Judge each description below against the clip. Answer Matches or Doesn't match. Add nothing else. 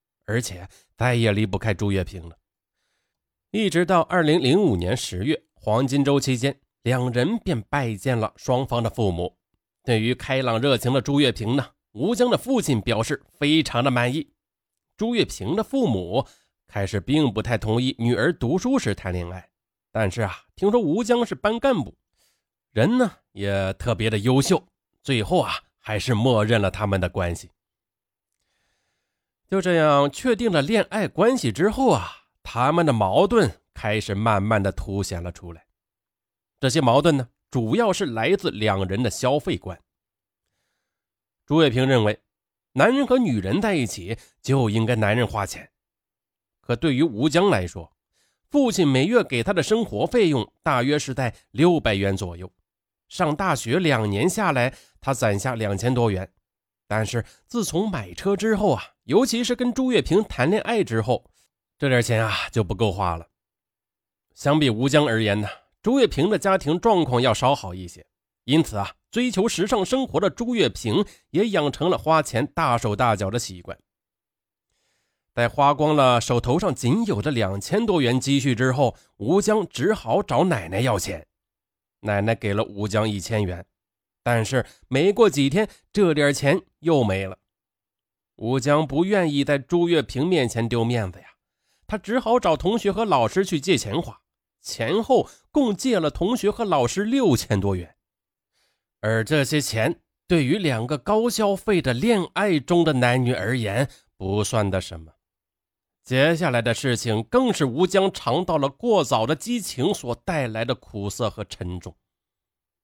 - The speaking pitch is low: Matches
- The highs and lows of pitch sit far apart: Matches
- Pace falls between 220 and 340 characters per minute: Matches